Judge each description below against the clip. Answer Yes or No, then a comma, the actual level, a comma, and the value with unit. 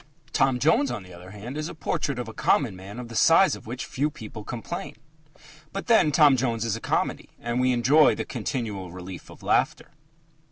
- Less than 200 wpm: No, fast, 205 wpm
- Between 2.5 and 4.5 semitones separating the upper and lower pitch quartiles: No, average, 5.2 semitones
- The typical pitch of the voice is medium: No, low, 120 Hz